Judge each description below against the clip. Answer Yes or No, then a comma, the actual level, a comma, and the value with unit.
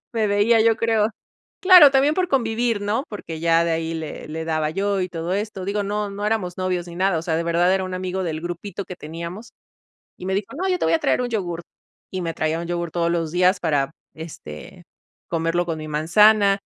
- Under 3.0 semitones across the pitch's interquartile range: No, average, 4.0 semitones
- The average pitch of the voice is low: No, medium, 185 Hz